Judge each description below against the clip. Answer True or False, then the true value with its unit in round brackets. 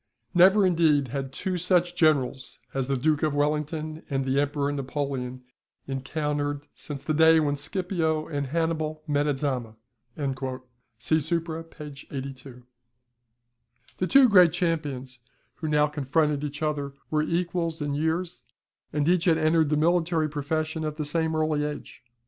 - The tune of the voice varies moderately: False (2.3 semitones)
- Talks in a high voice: False (150 Hz)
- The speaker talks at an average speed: True (150 wpm)